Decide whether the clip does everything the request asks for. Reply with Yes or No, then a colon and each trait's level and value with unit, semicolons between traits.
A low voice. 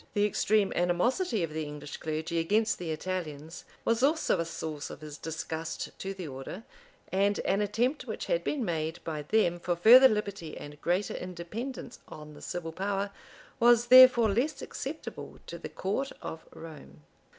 No: medium, 185 Hz